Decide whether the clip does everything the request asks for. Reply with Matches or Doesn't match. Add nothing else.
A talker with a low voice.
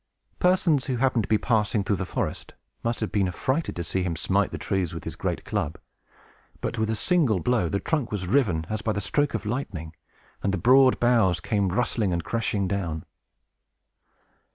Matches